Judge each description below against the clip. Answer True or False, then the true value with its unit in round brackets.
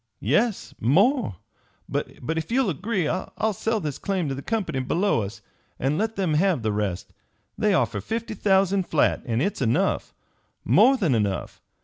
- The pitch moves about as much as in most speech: False (7.9 semitones)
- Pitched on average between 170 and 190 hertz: True (185 Hz)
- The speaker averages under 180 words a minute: True (160 wpm)